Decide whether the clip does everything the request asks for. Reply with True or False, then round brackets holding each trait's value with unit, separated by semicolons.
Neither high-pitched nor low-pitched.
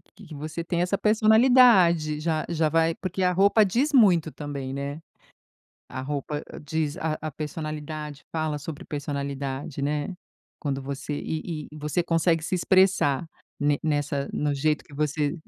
True (155 Hz)